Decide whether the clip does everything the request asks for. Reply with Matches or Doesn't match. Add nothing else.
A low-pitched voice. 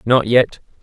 Matches